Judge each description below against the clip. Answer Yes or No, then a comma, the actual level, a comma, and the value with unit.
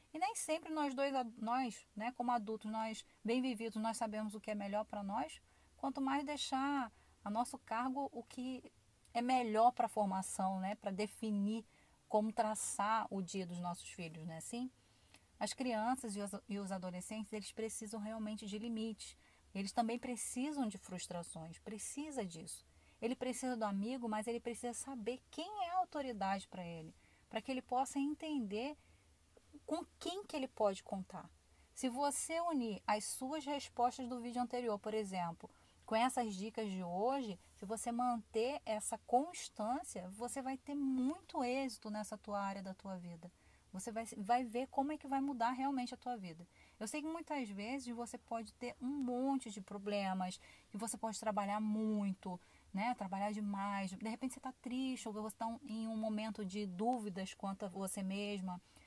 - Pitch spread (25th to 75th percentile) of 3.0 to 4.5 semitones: Yes, average, 3.8 semitones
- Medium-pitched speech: No, high, 225 Hz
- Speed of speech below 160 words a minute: No, average, 175 wpm